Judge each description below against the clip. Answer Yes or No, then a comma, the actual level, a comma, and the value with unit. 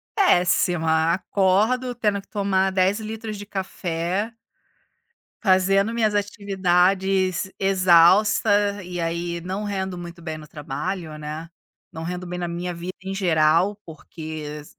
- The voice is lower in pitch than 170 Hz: No, medium, 185 Hz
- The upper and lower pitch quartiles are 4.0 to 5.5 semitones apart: No, average, 2.9 semitones